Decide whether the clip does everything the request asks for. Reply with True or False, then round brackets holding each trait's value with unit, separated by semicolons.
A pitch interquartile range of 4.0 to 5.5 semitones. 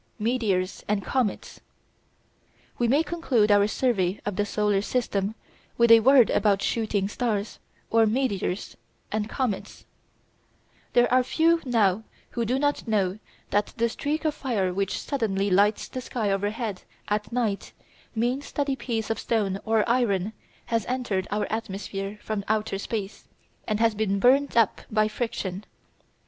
False (3.3 semitones)